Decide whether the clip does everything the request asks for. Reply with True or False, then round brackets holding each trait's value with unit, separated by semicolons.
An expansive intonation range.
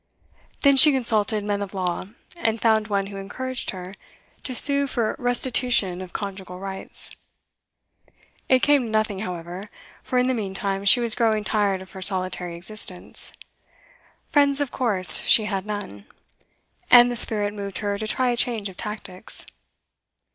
False (4.1 semitones)